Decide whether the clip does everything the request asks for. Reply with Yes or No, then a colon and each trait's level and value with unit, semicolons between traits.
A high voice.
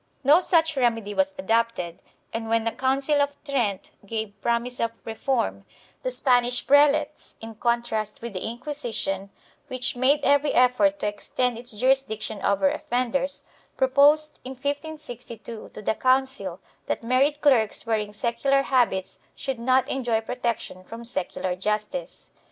Yes: high, 245 Hz